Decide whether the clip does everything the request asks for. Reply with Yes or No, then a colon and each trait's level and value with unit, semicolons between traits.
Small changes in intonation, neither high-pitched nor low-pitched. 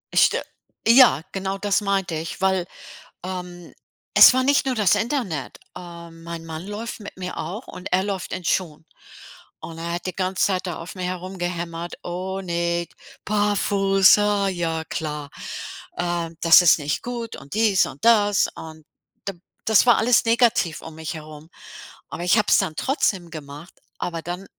No: average, 3.4 semitones; medium, 180 Hz